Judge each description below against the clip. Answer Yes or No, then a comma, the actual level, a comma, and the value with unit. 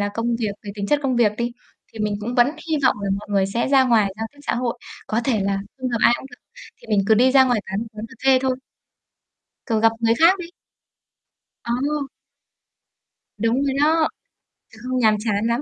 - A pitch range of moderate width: Yes, average, 3.4 semitones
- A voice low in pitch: No, high, 235 Hz